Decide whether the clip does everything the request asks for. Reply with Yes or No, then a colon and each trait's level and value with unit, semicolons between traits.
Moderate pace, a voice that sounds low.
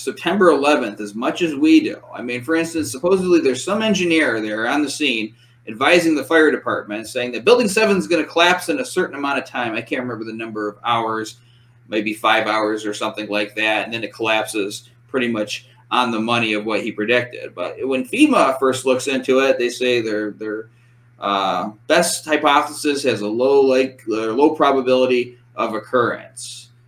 Yes: average, 195 wpm; low, 125 Hz